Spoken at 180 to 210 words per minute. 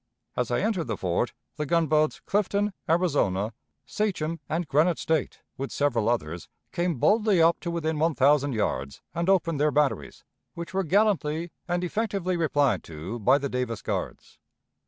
No: average, 155 wpm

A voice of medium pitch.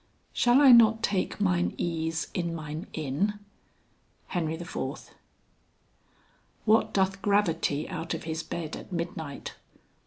Yes: medium, 175 Hz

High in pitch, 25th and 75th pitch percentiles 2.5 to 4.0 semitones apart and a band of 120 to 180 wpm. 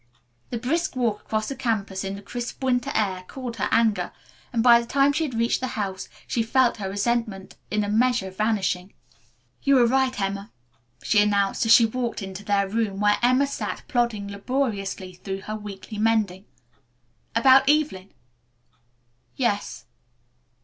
Yes: high, 220 Hz; average, 3.7 semitones; average, 160 wpm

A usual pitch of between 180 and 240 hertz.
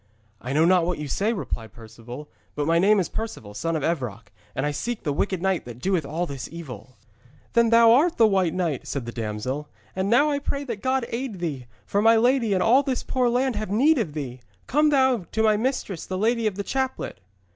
Yes: high, 190 Hz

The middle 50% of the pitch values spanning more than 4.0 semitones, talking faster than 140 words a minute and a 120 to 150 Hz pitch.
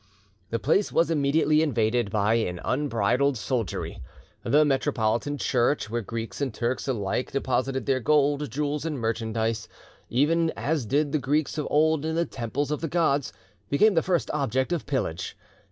Yes: average, 4.4 semitones; average, 160 wpm; medium, 140 Hz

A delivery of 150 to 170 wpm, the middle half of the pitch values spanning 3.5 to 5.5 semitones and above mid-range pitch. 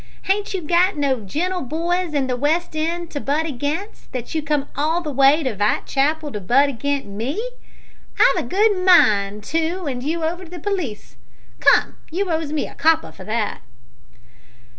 No: average, 180 wpm; average, 4.3 semitones; very high, 310 Hz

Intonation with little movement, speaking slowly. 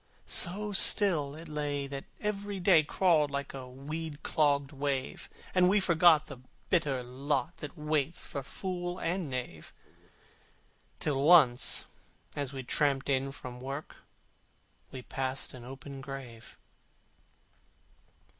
No: average, 3.9 semitones; slow, 125 wpm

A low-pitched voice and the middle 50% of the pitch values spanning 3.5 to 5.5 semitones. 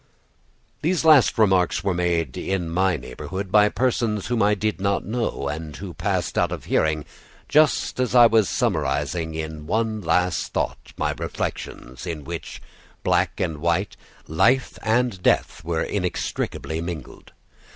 Yes: very low, 90 Hz; average, 5.2 semitones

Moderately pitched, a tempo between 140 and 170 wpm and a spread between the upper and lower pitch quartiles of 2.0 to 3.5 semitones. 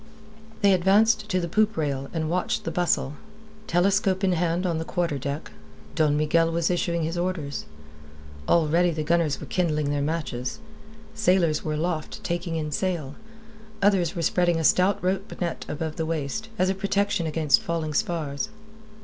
Yes: medium, 170 Hz; average, 165 wpm; average, 3.0 semitones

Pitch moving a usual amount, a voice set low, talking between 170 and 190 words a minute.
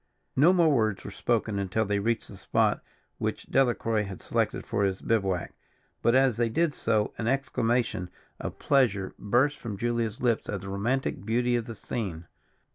Yes: average, 3.5 semitones; low, 115 Hz; average, 175 wpm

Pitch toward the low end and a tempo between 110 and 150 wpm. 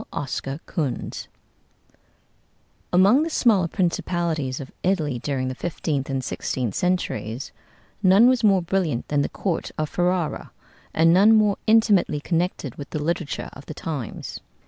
No: medium, 165 Hz; average, 140 wpm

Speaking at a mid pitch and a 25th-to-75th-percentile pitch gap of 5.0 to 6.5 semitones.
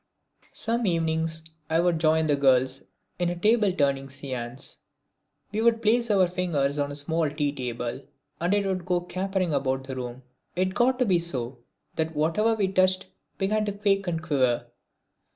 Yes: medium, 165 Hz; wide, 5.6 semitones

